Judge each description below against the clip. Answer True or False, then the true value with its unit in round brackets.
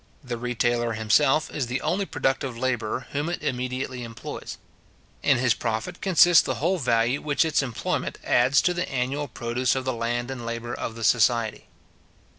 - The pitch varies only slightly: False (3.2 semitones)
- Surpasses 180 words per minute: False (170 wpm)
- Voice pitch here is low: True (125 Hz)